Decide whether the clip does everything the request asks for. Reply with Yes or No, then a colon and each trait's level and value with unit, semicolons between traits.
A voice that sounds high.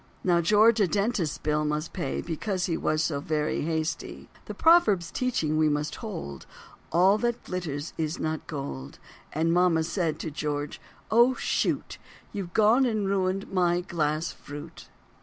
No: medium, 170 Hz